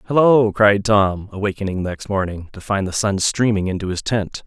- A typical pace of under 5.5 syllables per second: Yes, 5.2 syllables/s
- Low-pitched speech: Yes, low, 100 Hz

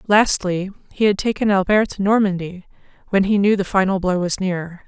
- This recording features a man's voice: No, female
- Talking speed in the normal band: Yes, average, 185 wpm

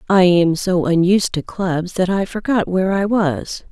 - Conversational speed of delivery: Yes, average, 195 wpm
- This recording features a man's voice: No, female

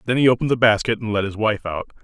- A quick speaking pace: Yes, fast, 295 wpm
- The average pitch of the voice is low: Yes, low, 110 Hz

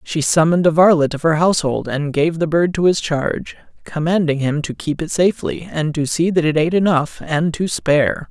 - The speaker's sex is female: No, male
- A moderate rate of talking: No, fast, 215 wpm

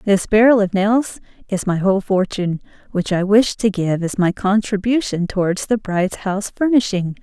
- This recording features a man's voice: No, female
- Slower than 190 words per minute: Yes, average, 175 wpm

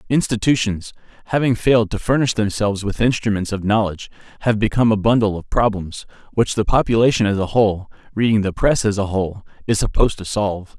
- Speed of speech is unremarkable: Yes, average, 180 wpm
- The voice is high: No, low, 105 Hz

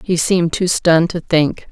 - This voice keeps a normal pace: No, fast, 210 wpm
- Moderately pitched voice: Yes, medium, 170 Hz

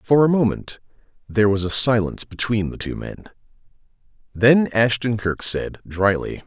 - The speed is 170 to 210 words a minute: No, average, 150 wpm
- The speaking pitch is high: No, low, 110 Hz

